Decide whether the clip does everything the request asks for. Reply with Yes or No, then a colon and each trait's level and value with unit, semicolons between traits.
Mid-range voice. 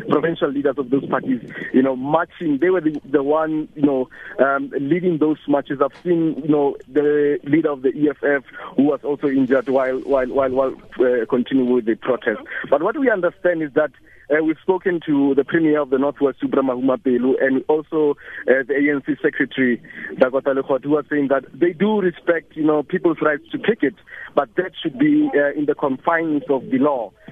Yes: medium, 145 Hz